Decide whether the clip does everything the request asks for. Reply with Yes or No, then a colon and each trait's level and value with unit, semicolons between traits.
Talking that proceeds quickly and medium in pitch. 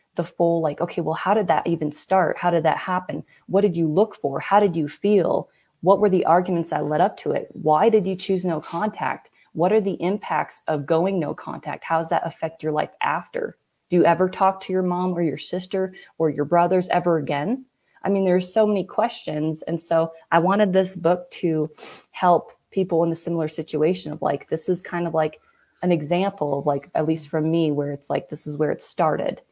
Yes: fast, 225 wpm; medium, 170 Hz